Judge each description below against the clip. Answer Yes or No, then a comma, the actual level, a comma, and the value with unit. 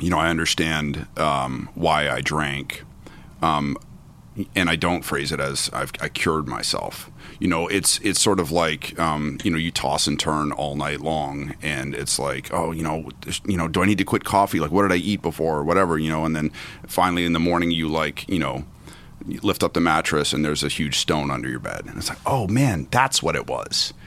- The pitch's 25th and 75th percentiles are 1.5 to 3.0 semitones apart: Yes, narrow, 2.5 semitones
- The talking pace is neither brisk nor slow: No, fast, 230 wpm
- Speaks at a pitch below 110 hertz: Yes, very low, 80 Hz